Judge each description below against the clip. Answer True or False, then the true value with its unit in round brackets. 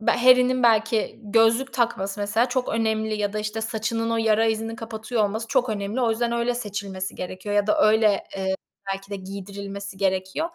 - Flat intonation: True (2.3 semitones)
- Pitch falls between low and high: False (220 Hz)